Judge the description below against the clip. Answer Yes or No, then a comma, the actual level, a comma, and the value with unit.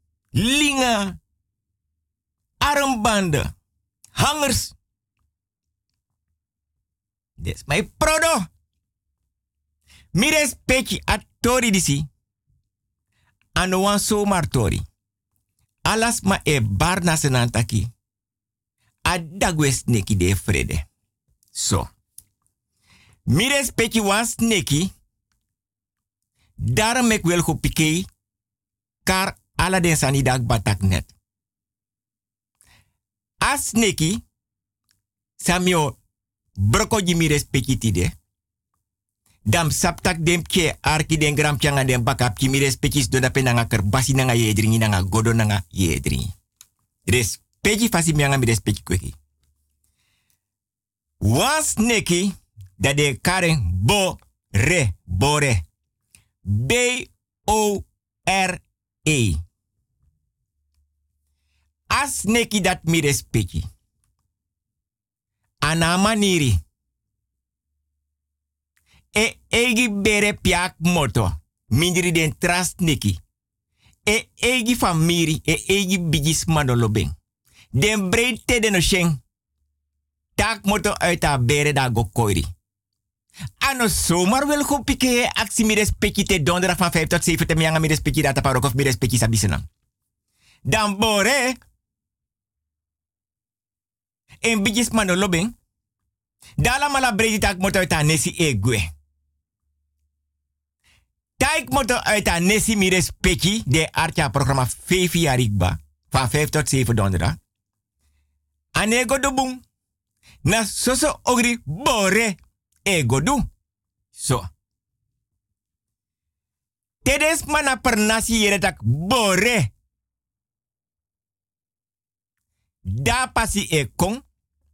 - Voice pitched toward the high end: No, low, 120 Hz